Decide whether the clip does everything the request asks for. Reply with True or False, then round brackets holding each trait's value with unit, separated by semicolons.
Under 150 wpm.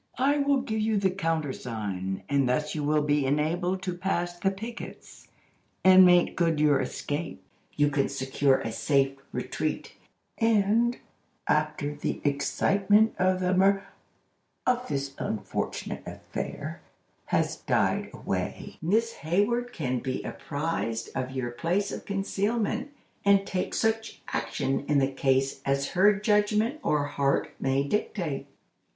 True (135 wpm)